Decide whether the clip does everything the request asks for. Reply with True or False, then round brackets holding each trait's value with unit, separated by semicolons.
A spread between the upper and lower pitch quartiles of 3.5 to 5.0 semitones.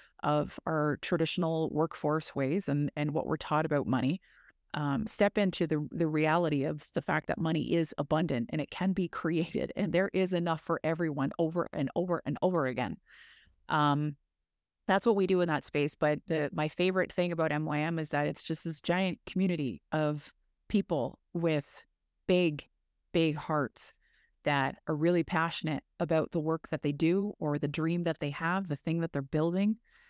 False (2.7 semitones)